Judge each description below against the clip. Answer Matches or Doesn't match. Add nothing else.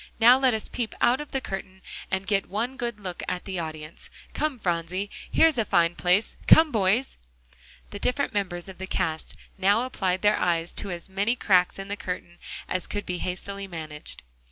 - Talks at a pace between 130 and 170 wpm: Doesn't match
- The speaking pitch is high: Matches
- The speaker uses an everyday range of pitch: Matches